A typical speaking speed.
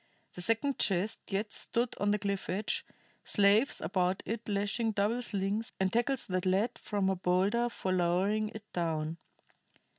Yes: average, 155 wpm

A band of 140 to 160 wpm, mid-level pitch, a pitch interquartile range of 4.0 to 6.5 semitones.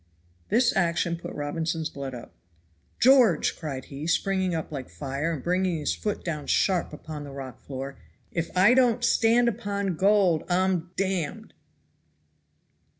Yes: average, 150 wpm; medium, 170 Hz; average, 4.8 semitones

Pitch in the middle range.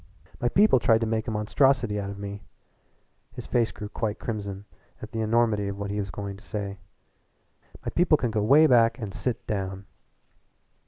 No: low, 110 Hz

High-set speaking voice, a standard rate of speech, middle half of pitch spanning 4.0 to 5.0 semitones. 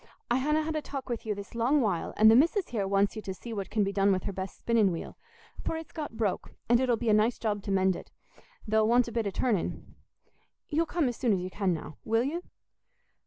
No: high, 225 Hz; fast, 250 wpm; average, 4.4 semitones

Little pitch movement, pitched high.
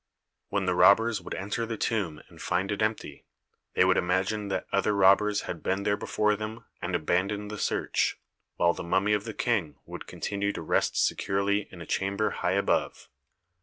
No: narrow, 2.0 semitones; low, 100 Hz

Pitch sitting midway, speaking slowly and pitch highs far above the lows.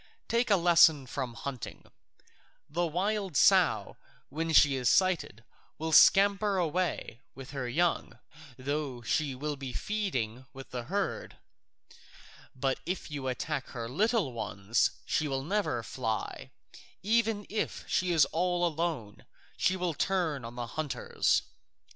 Yes: medium, 155 Hz; slow, 130 wpm; wide, 6.0 semitones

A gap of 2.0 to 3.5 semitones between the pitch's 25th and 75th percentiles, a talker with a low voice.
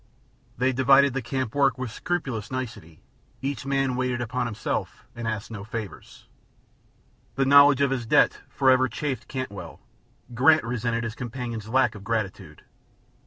Yes: average, 2.9 semitones; low, 125 Hz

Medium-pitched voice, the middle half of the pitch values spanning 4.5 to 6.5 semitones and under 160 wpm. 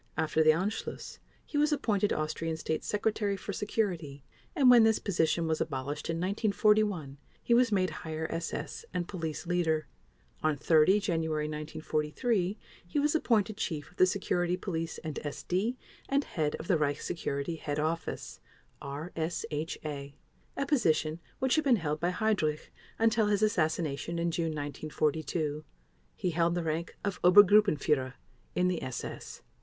Yes: medium, 170 Hz; average, 4.8 semitones; average, 150 wpm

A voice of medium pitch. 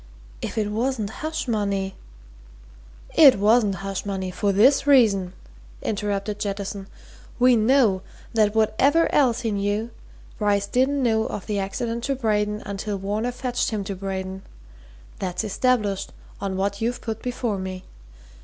No: high, 210 Hz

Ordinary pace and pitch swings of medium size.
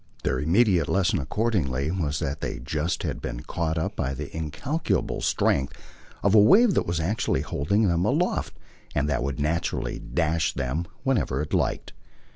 No: average, 165 wpm; wide, 5.9 semitones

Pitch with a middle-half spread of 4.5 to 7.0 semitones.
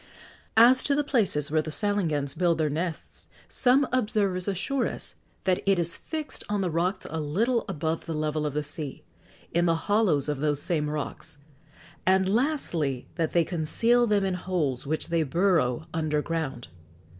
Yes: average, 5.0 semitones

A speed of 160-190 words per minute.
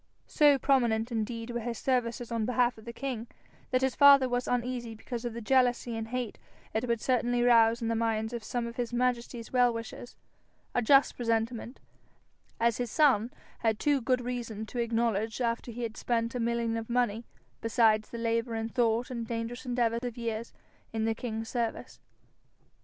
Yes: average, 185 wpm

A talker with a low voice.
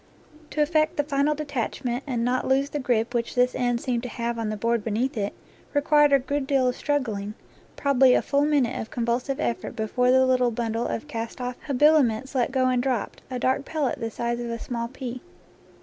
No: very high, 250 Hz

